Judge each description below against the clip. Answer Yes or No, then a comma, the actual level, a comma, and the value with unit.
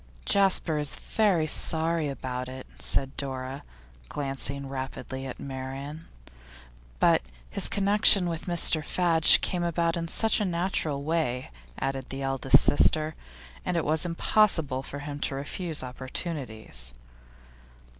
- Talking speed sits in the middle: No, slow, 125 wpm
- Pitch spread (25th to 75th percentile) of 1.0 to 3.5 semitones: No, average, 4.0 semitones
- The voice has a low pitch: No, medium, 145 Hz